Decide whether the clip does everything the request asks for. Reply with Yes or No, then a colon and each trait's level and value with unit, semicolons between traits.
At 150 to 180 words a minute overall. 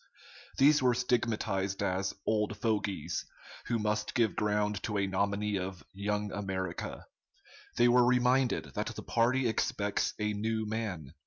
No: average, 140 wpm